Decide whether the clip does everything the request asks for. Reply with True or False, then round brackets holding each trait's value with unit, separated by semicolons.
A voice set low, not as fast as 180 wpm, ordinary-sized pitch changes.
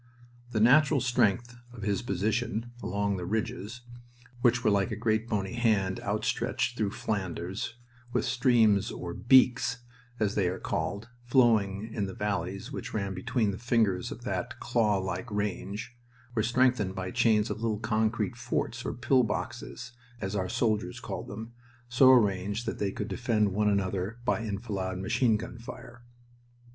True (110 Hz; 155 wpm; 3.2 semitones)